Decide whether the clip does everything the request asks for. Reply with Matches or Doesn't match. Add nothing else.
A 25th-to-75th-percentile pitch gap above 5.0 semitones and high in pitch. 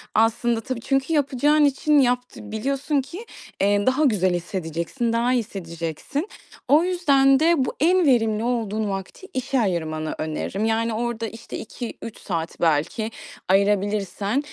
Matches